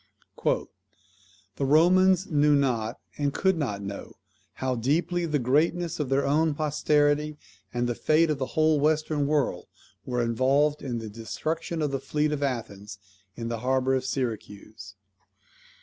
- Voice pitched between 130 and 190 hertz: Yes, medium, 140 Hz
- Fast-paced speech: No, average, 150 wpm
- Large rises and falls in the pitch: No, average, 4.0 semitones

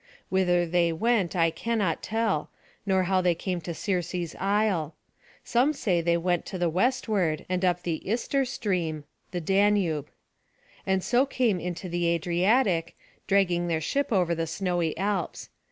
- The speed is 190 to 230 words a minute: No, average, 150 wpm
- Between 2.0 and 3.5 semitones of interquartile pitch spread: Yes, average, 3.2 semitones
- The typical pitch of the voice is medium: Yes, medium, 180 Hz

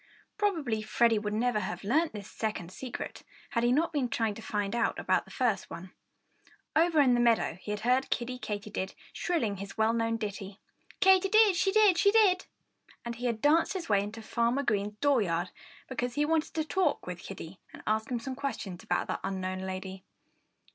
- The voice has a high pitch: Yes, high, 230 Hz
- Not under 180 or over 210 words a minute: Yes, average, 200 wpm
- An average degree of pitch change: No, wide, 6.0 semitones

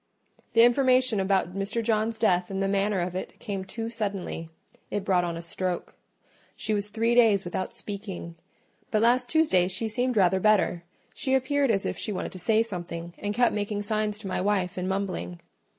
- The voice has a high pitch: Yes, high, 205 Hz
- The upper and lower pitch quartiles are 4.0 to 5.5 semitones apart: No, average, 3.4 semitones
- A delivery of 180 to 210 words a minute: Yes, average, 190 wpm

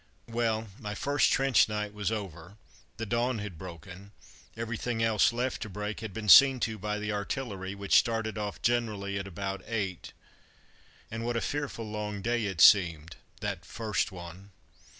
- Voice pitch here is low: Yes, low, 105 Hz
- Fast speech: No, average, 165 wpm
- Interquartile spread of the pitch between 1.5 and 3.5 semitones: Yes, average, 2.7 semitones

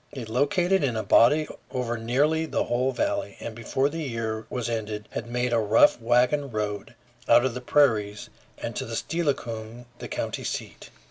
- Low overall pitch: Yes, low, 120 Hz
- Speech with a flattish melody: No, average, 4.2 semitones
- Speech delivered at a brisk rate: No, average, 175 wpm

